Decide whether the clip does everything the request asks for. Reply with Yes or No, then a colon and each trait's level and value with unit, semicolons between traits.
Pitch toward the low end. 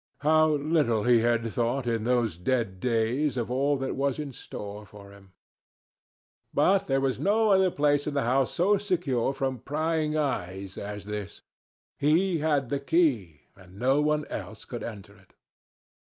Yes: low, 130 Hz